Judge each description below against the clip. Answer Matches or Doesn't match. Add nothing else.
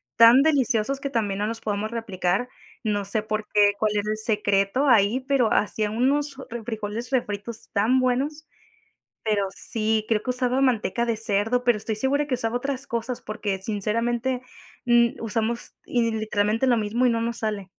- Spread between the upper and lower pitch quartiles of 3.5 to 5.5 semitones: Doesn't match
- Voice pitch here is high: Matches